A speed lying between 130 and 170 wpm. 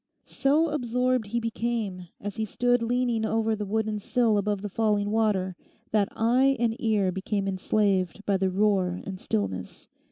Yes: average, 160 wpm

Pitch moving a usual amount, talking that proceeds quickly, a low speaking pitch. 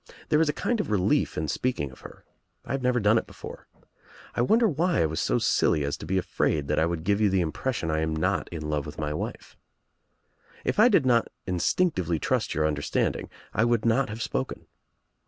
No: wide, 8.5 semitones; fast, 215 wpm; low, 100 Hz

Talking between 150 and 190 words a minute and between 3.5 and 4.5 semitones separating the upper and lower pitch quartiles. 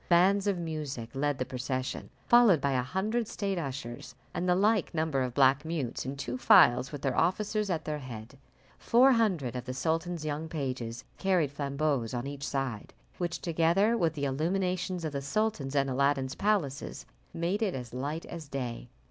No: average, 180 wpm; wide, 5.4 semitones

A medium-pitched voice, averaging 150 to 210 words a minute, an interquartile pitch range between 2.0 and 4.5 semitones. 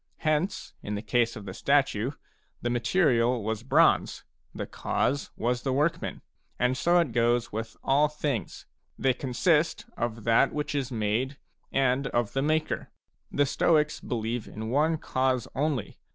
No: low, 130 Hz; average, 155 wpm; average, 4.0 semitones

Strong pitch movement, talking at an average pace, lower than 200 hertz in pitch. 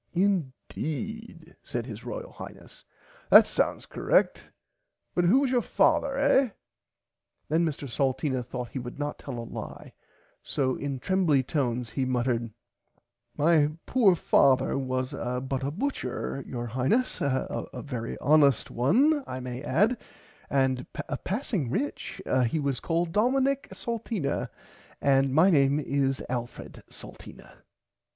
No: wide, 6.7 semitones; slow, 130 wpm; medium, 140 Hz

